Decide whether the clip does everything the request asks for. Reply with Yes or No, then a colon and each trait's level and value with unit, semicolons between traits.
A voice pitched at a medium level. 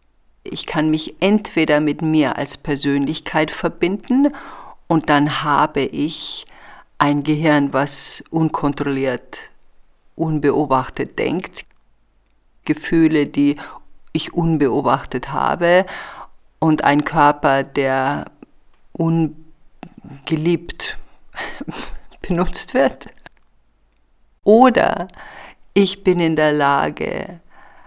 Yes: medium, 155 Hz